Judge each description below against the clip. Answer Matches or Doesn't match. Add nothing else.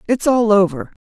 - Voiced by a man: Doesn't match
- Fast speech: Doesn't match